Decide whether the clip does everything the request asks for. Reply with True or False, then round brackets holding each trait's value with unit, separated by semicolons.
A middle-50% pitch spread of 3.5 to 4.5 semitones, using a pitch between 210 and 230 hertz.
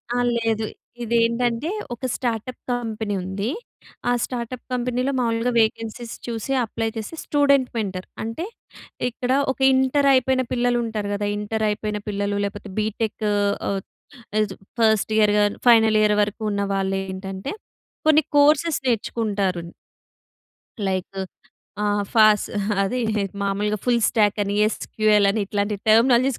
False (2.9 semitones; 220 Hz)